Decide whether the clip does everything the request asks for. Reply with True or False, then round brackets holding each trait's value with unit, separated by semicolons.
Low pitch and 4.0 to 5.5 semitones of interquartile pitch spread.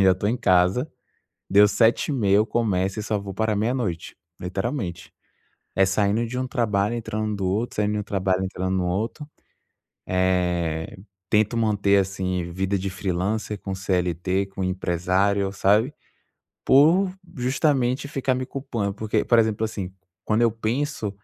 False (100 Hz; 3.5 semitones)